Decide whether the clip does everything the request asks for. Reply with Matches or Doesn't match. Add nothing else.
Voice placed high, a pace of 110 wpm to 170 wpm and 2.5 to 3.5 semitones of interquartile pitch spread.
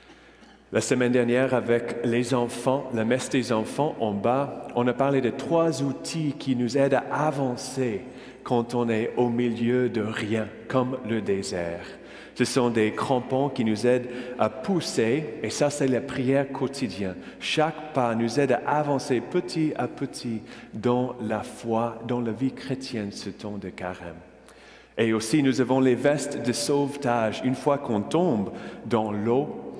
Doesn't match